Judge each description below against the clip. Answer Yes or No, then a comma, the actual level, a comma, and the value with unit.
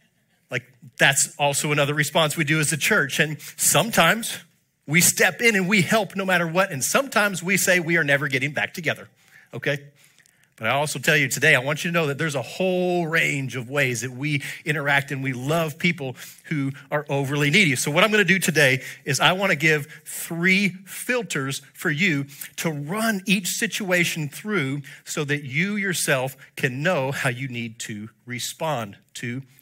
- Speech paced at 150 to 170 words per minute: No, average, 185 wpm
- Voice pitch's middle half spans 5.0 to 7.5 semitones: No, average, 4.3 semitones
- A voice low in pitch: No, medium, 150 Hz